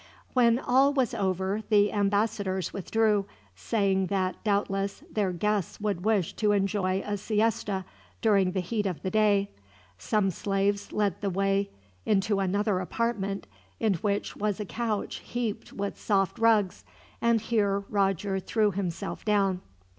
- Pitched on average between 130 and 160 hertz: No, high, 200 Hz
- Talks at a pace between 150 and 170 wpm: No, average, 140 wpm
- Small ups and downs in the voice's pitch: Yes, narrow, 1.7 semitones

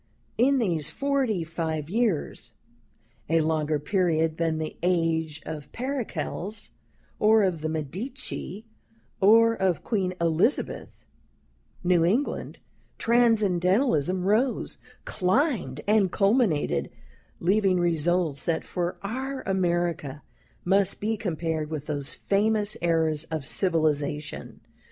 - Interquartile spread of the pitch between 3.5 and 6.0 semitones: Yes, average, 5.1 semitones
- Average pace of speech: No, slow, 105 wpm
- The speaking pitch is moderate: Yes, medium, 180 Hz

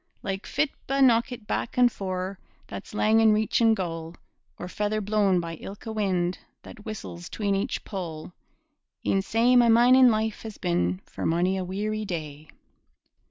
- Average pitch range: Yes, average, 3.8 semitones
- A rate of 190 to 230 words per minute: No, average, 155 wpm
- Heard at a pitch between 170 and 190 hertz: No, high, 205 Hz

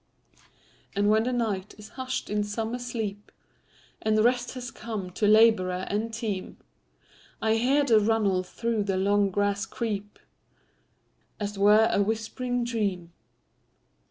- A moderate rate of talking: No, slow, 125 wpm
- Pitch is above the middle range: Yes, high, 215 Hz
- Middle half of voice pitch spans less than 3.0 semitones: Yes, narrow, 2.5 semitones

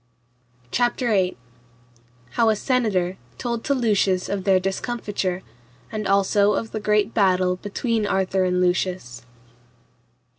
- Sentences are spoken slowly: Yes, slow, 120 wpm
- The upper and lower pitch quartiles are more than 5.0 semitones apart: No, average, 3.2 semitones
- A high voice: Yes, high, 200 Hz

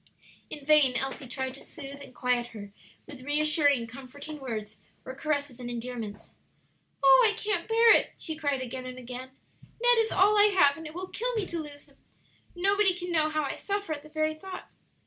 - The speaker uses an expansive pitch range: Yes, wide, 5.7 semitones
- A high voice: Yes, very high, 290 Hz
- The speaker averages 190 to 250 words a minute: Yes, average, 200 wpm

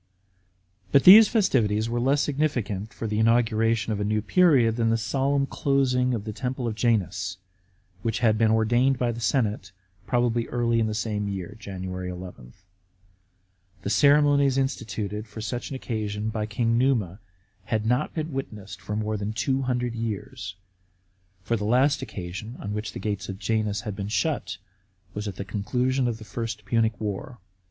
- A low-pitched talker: Yes, low, 110 Hz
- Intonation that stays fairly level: No, average, 3.3 semitones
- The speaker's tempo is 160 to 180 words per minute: Yes, average, 170 wpm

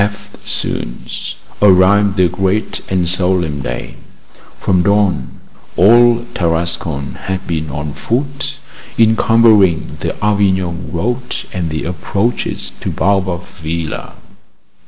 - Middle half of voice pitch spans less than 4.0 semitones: Yes, average, 3.6 semitones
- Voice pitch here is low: Yes, very low, 95 Hz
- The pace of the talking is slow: Yes, slow, 100 wpm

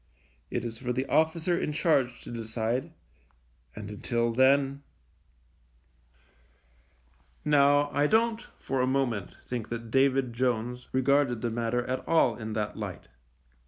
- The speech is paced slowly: Yes, slow, 130 wpm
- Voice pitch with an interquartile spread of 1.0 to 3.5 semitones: Yes, average, 3.1 semitones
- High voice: No, low, 125 Hz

